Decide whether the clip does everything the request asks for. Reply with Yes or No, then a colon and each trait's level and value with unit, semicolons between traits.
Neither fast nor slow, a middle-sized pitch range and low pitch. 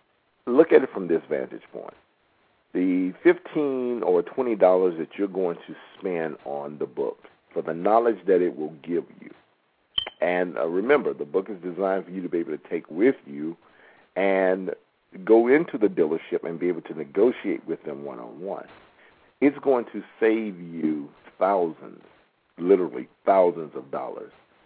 Yes: average, 165 wpm; average, 3.9 semitones; very low, 95 Hz